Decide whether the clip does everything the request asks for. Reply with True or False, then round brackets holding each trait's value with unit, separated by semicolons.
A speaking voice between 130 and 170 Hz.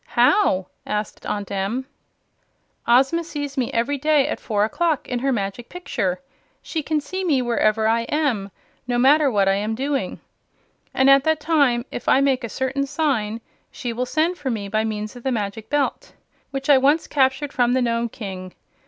False (255 Hz)